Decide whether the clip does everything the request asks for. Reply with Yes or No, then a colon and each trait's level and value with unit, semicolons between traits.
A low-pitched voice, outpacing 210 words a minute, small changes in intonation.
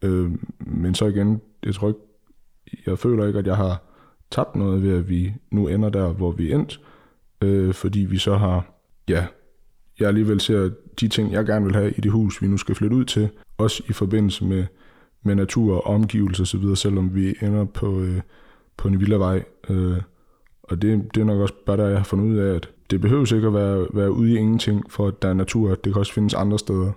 Yes: low, 100 Hz; fast, 225 wpm; narrow, 2.0 semitones